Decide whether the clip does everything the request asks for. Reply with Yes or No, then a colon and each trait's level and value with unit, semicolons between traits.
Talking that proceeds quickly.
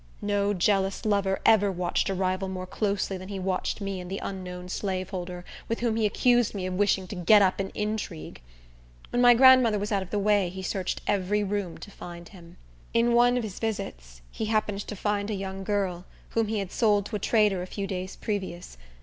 Yes: fast, 210 wpm